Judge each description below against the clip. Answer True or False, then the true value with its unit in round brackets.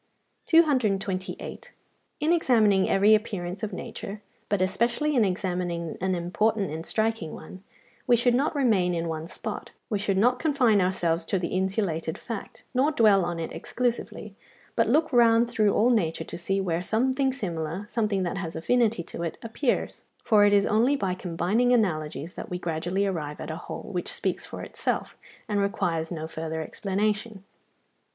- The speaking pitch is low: False (200 Hz)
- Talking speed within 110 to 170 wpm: True (165 wpm)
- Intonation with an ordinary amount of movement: True (4.7 semitones)